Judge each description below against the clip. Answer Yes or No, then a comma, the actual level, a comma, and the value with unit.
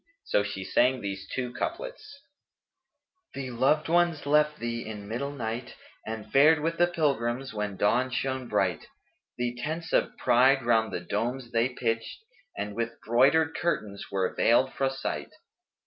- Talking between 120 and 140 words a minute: No, average, 160 wpm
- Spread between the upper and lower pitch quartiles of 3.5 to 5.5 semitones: Yes, average, 4.6 semitones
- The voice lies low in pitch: Yes, low, 125 Hz